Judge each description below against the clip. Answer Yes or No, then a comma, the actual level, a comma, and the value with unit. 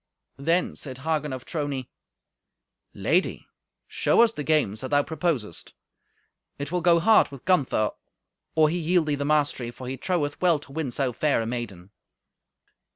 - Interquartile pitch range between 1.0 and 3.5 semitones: No, average, 4.1 semitones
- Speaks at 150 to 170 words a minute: Yes, average, 160 wpm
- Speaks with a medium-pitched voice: Yes, medium, 145 Hz